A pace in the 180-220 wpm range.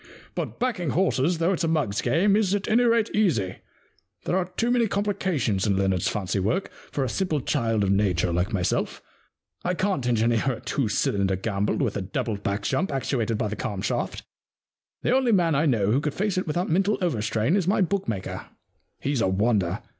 Yes: average, 200 wpm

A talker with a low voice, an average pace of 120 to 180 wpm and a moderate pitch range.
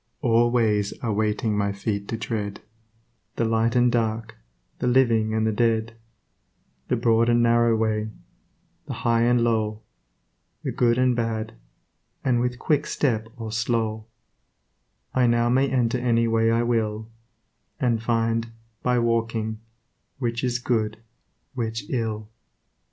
No: low, 115 Hz; average, 140 wpm; narrow, 1.5 semitones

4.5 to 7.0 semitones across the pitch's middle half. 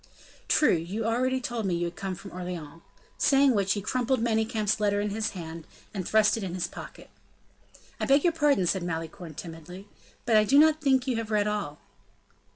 Yes: average, 5.2 semitones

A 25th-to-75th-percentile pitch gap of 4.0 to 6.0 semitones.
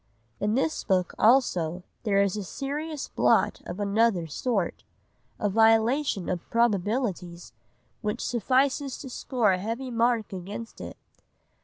Yes: average, 4.7 semitones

